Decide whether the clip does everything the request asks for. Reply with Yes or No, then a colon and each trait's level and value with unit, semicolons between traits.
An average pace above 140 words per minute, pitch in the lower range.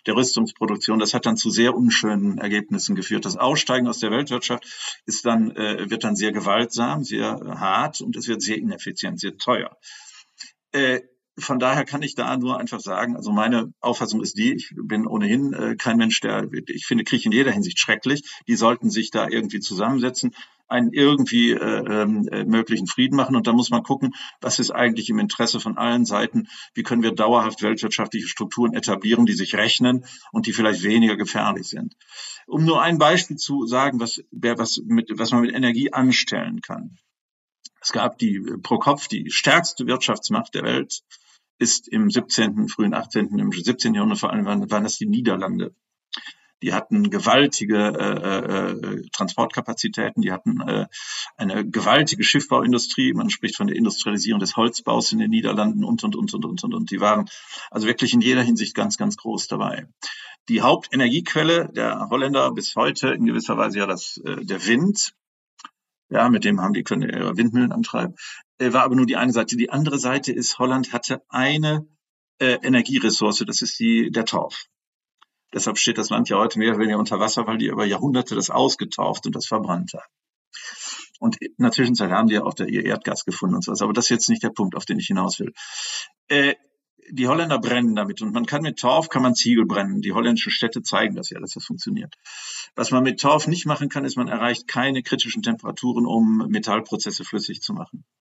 Yes: fast, 190 wpm; low, 130 Hz